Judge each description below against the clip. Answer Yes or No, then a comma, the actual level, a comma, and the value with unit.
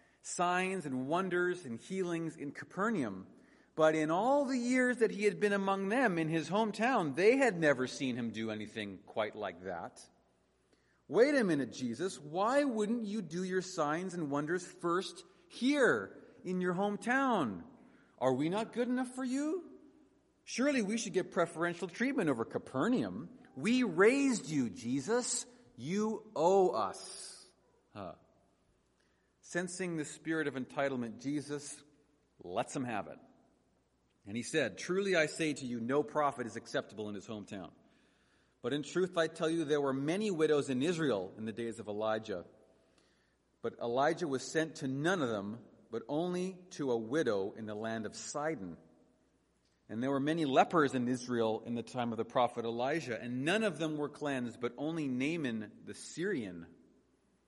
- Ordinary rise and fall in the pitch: No, wide, 8.4 semitones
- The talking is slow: No, average, 165 wpm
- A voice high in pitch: No, medium, 160 Hz